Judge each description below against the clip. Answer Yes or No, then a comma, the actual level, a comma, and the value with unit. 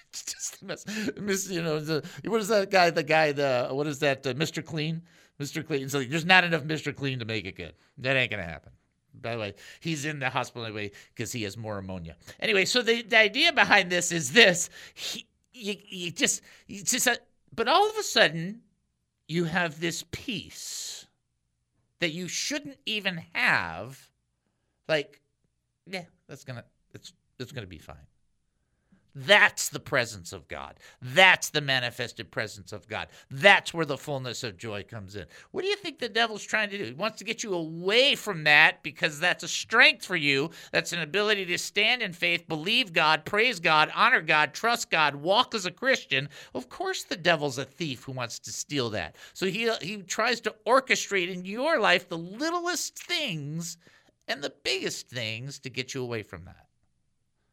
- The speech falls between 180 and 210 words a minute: Yes, average, 190 wpm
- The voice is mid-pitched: Yes, medium, 165 Hz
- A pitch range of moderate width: No, wide, 8.0 semitones